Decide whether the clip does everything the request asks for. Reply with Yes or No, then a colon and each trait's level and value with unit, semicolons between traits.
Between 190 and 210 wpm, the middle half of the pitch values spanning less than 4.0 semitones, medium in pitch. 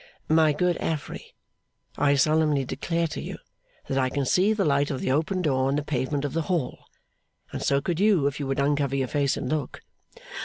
Yes: fast, 205 wpm; average, 2.8 semitones; medium, 145 Hz